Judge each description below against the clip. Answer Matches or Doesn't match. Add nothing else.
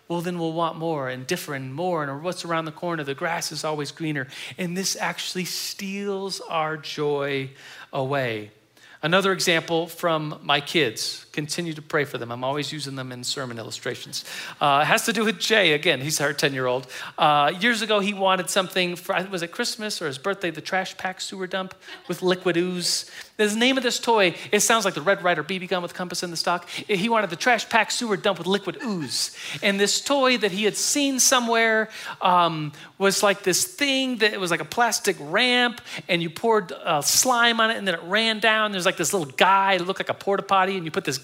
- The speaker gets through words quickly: Matches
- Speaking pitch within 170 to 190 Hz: Matches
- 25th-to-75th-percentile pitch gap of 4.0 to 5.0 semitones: Matches